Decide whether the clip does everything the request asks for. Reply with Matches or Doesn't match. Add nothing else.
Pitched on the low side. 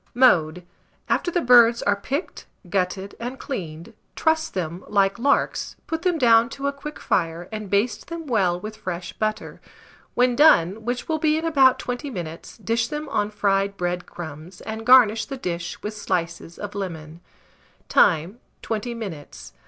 Doesn't match